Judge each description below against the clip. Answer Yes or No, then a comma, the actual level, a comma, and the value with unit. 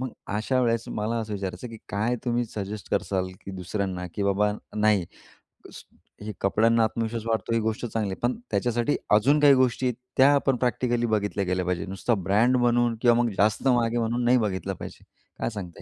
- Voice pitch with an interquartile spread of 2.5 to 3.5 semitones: Yes, average, 3.0 semitones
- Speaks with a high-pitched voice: No, low, 115 Hz